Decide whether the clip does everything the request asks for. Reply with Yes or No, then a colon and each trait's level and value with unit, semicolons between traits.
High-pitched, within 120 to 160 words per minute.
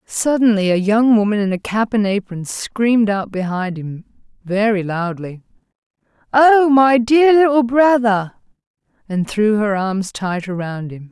Yes: high, 215 Hz; average, 145 wpm